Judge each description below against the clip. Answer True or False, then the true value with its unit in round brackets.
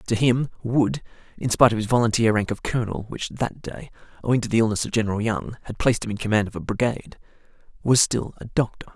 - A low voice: True (115 Hz)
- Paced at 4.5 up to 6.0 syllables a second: False (6.6 syllables/s)